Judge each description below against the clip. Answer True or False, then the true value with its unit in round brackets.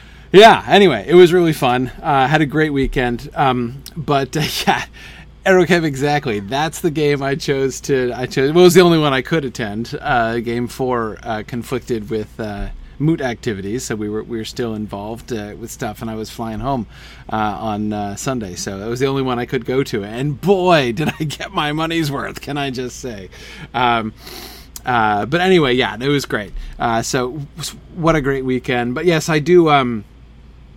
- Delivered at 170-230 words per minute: True (205 wpm)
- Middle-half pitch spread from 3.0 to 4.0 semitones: False (4.6 semitones)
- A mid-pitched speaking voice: False (130 Hz)